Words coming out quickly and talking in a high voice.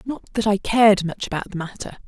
Yes: fast, 230 wpm; high, 205 Hz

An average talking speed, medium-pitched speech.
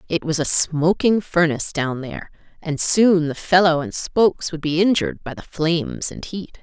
Yes: average, 190 wpm; medium, 165 Hz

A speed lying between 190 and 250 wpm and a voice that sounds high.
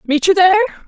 Yes: fast, 205 wpm; very high, 370 Hz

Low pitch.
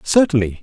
No: medium, 150 Hz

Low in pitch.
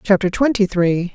No: high, 195 Hz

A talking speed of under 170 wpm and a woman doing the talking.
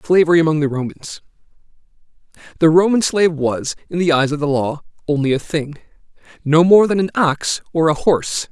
No: average, 160 wpm; male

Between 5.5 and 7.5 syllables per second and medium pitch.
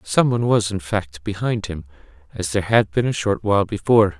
No: 5.9 syllables/s; low, 105 Hz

